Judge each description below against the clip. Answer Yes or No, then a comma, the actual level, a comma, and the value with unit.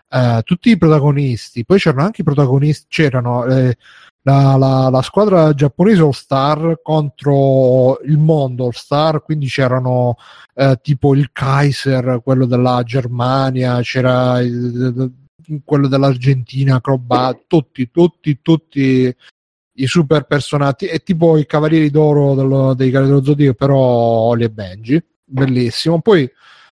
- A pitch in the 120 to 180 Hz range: Yes, low, 135 Hz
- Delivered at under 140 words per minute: Yes, average, 130 wpm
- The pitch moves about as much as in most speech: Yes, average, 3.0 semitones